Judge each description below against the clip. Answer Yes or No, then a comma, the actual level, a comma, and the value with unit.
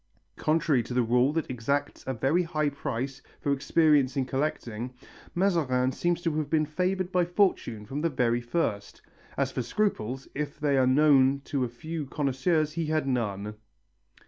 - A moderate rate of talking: Yes, average, 170 wpm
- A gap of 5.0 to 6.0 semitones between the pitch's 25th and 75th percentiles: No, average, 3.9 semitones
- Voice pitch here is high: No, medium, 140 Hz